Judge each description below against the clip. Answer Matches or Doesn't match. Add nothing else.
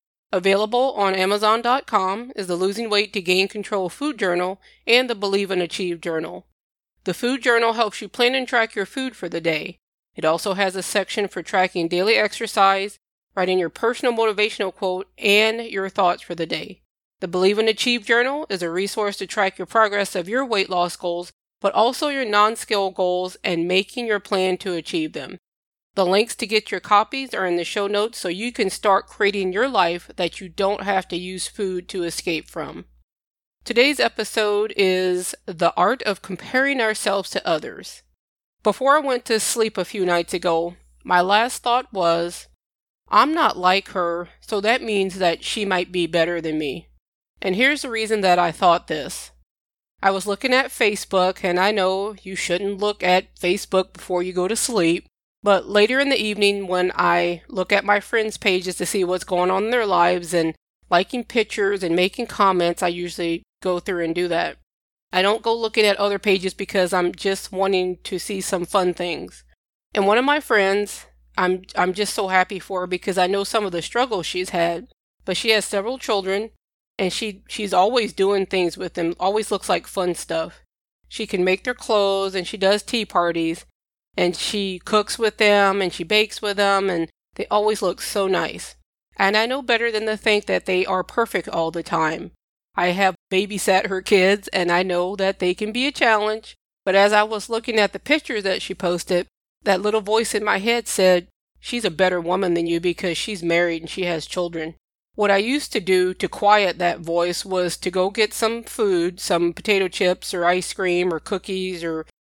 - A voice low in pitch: Doesn't match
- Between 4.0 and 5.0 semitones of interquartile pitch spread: Doesn't match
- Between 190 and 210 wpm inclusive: Matches